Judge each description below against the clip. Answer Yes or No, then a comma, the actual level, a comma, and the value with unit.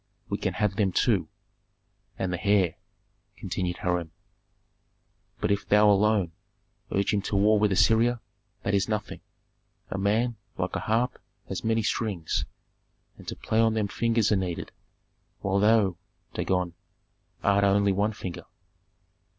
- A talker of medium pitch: No, low, 100 Hz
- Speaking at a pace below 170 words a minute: Yes, average, 140 wpm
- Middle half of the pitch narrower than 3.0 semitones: Yes, narrow, 2.4 semitones